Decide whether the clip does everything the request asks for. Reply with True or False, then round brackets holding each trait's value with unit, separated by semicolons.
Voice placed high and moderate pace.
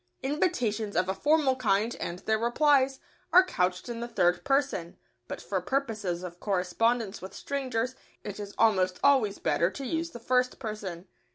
True (225 Hz; 165 wpm)